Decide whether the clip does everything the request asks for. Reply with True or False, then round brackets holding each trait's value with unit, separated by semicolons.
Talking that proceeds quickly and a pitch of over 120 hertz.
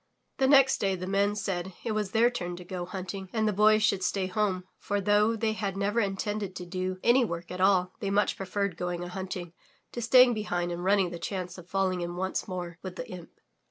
True (230 wpm; 190 Hz)